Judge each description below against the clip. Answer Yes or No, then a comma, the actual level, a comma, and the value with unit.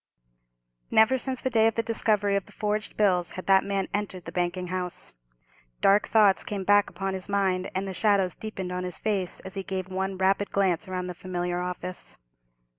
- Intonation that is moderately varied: No, narrow, 2.1 semitones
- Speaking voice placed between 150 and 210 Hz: Yes, high, 190 Hz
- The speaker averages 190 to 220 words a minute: Yes, average, 195 wpm